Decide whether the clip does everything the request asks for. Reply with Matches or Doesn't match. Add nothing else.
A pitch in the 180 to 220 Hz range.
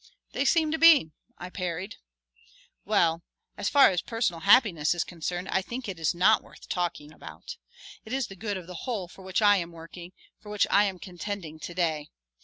Matches